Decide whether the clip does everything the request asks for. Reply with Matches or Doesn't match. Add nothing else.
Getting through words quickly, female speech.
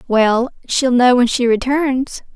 Doesn't match